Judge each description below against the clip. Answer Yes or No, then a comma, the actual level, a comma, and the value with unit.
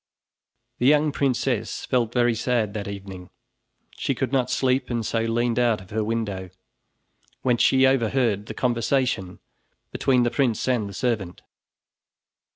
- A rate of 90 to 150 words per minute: Yes, average, 145 wpm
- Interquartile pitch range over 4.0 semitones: No, average, 3.2 semitones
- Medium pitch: No, low, 120 Hz